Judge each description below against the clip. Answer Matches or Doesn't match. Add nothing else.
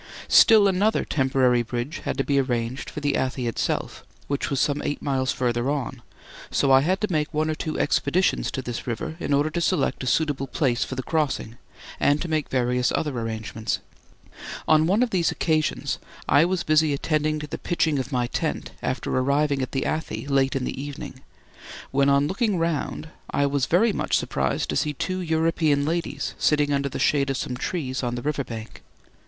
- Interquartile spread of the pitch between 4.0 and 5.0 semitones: Doesn't match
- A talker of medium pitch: Matches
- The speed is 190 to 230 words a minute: Matches